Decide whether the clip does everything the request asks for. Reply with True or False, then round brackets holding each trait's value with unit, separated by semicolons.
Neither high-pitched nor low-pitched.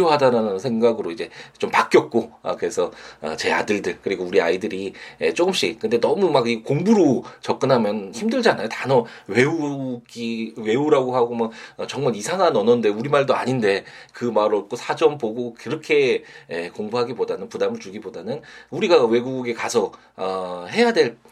True (145 Hz)